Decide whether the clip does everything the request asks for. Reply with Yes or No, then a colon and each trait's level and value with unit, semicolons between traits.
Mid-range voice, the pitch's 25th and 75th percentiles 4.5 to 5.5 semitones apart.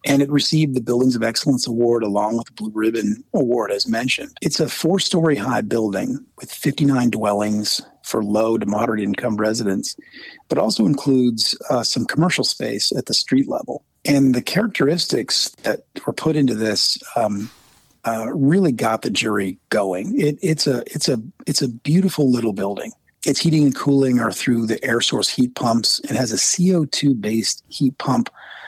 No: low, 125 Hz; average, 4.8 semitones